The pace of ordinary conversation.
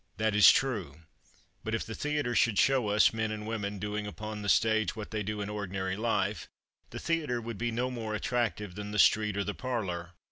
No: fast, 210 wpm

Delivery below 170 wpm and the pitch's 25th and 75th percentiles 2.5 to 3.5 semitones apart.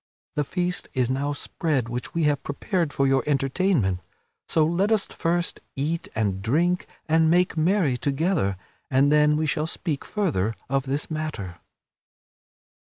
No: average, 150 wpm; average, 4.0 semitones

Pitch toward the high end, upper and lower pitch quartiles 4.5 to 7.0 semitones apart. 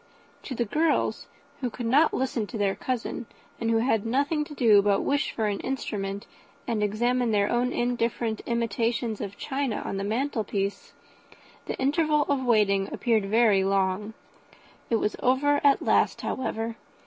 No: high, 230 Hz; average, 3.8 semitones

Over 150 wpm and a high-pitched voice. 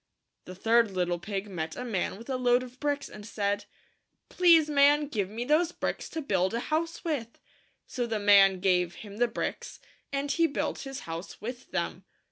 Yes: average, 195 wpm; high, 230 Hz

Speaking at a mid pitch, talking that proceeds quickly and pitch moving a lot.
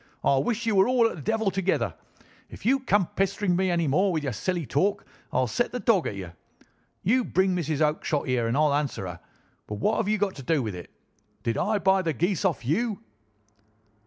Yes: medium, 180 Hz; fast, 215 wpm; wide, 6.4 semitones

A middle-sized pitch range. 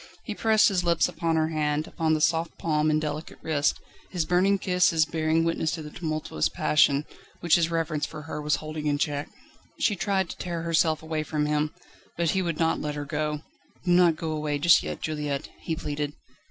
No: narrow, 1.9 semitones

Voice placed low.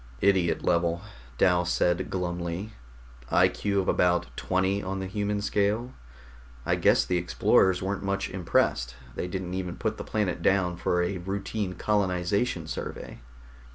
Yes: very low, 95 Hz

